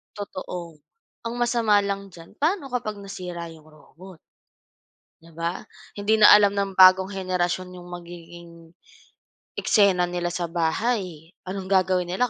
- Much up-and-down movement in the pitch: No, average, 2.8 semitones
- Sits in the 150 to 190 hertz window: Yes, medium, 185 Hz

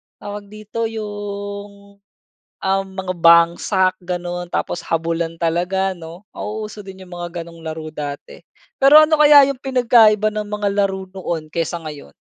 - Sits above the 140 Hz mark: Yes, high, 190 Hz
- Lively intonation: No, average, 3.8 semitones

